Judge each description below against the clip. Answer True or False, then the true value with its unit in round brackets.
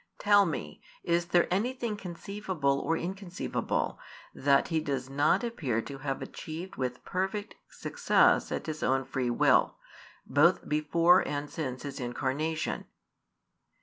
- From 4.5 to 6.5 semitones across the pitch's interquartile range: True (5.2 semitones)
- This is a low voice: False (155 Hz)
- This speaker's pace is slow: True (130 wpm)